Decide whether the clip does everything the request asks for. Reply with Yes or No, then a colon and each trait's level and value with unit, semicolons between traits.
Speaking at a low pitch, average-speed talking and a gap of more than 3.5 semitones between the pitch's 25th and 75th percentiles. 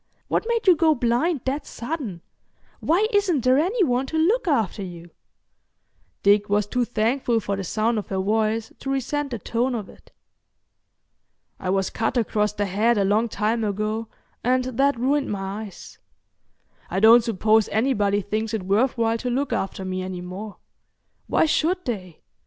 No: high, 225 Hz; average, 170 wpm; average, 4.7 semitones